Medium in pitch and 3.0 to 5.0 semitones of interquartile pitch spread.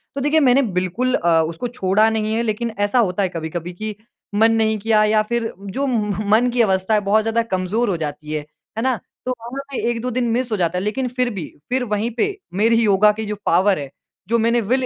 No: high, 220 Hz; average, 3.8 semitones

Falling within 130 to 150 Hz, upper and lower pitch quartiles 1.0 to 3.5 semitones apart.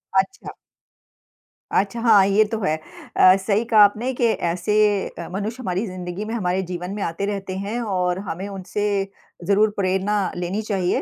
No: high, 195 Hz; narrow, 2.6 semitones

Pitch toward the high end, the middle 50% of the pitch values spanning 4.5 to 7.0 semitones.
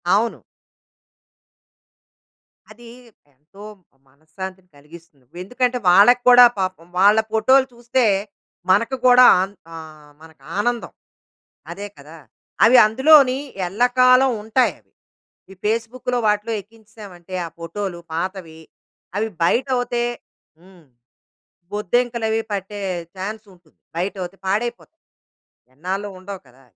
Yes: high, 205 Hz; average, 5.1 semitones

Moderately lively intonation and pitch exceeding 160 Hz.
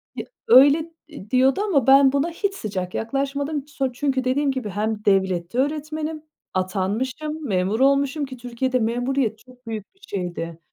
Yes: average, 5.0 semitones; very high, 260 Hz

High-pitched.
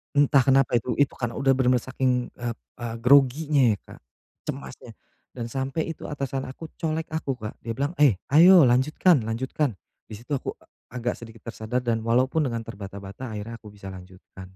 No: low, 125 Hz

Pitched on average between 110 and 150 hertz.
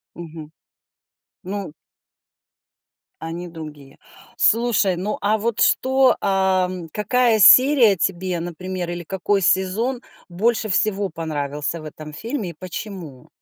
No: medium, 185 Hz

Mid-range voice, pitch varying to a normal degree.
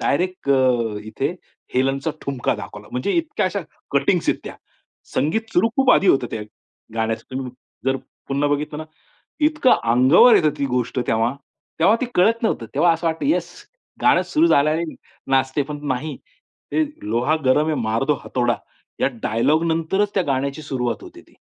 No: medium, 145 Hz; wide, 5.7 semitones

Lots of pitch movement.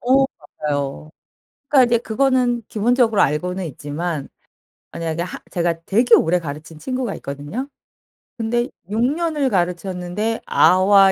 Yes: wide, 6.6 semitones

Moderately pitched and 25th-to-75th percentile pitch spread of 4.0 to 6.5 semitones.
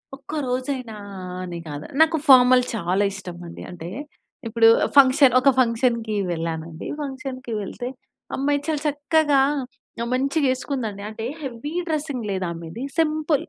No: very high, 255 Hz; wide, 5.6 semitones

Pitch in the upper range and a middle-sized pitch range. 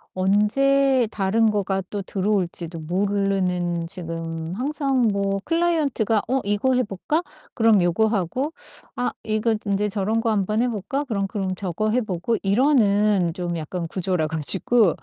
Yes: high, 205 Hz; average, 3.9 semitones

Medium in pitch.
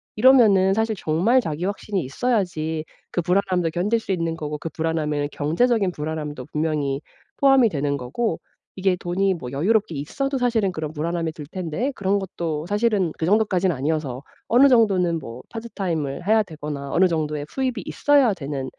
Yes: medium, 175 Hz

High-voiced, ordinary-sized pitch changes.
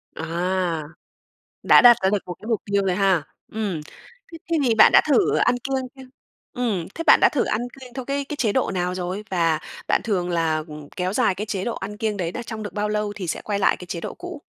Yes: high, 200 Hz; average, 4.7 semitones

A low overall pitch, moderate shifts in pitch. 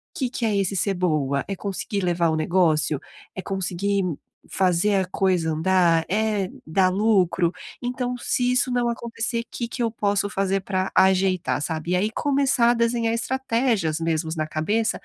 No: high, 195 Hz; average, 4.8 semitones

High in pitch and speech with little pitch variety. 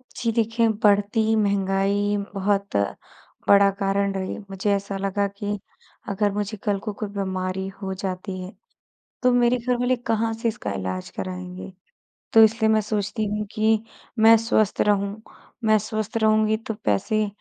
Yes: high, 205 Hz; narrow, 2.0 semitones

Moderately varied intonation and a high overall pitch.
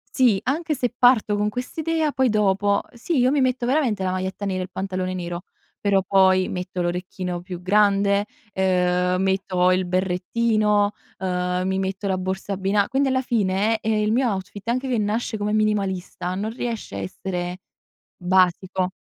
Yes: average, 3.2 semitones; high, 195 Hz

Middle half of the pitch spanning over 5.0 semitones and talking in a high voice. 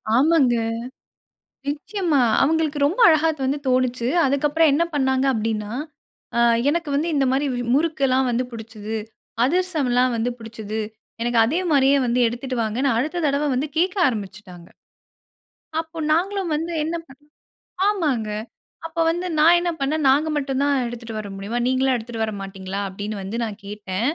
Yes: wide, 5.4 semitones; very high, 265 Hz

